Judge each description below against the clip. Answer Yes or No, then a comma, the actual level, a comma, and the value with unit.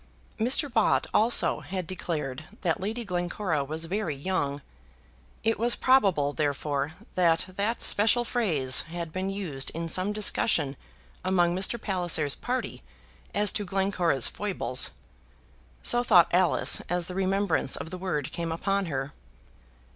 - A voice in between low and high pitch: Yes, medium, 180 Hz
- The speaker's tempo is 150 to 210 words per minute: No, slow, 135 wpm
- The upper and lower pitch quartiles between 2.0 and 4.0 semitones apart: No, average, 4.5 semitones